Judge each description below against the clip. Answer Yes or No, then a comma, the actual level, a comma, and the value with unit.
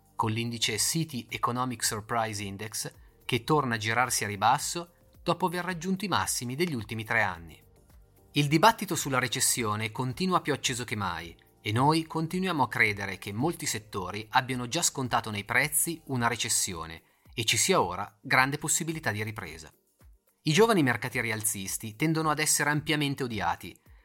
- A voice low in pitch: Yes, low, 125 Hz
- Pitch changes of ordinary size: No, wide, 6.1 semitones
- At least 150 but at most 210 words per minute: Yes, average, 155 wpm